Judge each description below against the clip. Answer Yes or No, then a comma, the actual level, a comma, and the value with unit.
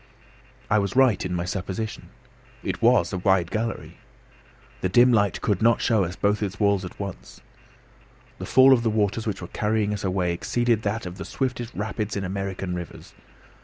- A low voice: Yes, low, 100 Hz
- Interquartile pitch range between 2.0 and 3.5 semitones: Yes, average, 3.1 semitones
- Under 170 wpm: No, average, 185 wpm